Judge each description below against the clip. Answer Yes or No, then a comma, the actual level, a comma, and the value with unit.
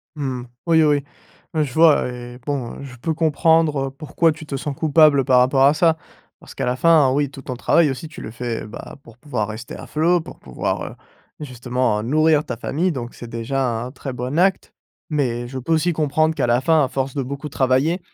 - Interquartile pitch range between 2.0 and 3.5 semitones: No, average, 3.9 semitones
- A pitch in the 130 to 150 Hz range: Yes, medium, 140 Hz